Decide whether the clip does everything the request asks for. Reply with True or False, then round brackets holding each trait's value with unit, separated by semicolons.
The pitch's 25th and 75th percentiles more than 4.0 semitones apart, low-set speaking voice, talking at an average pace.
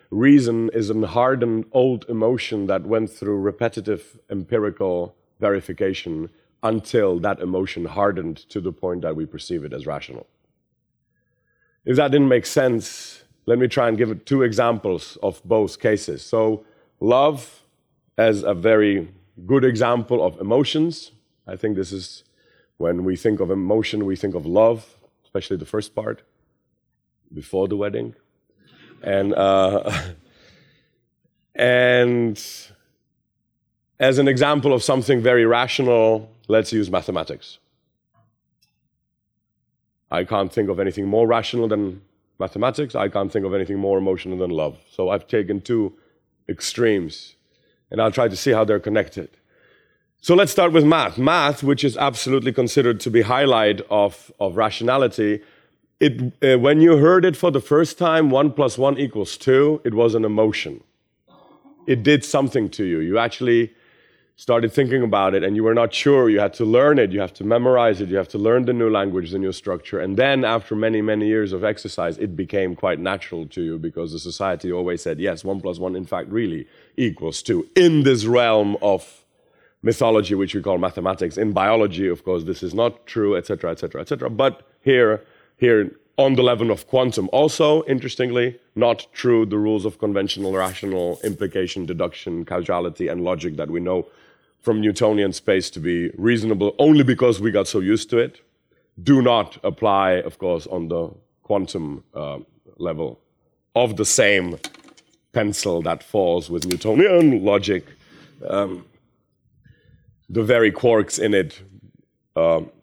True (4.5 semitones; 110 Hz; 160 wpm)